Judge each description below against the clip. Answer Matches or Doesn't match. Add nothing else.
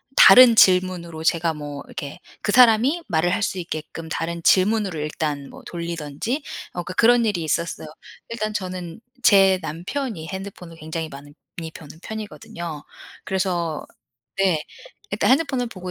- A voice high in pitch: Doesn't match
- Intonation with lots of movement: Doesn't match